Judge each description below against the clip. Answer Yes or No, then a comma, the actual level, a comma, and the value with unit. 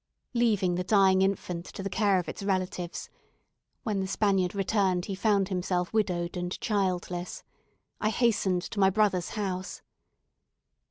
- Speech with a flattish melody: Yes, narrow, 2.0 semitones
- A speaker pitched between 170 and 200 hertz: Yes, high, 190 Hz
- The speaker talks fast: No, average, 145 wpm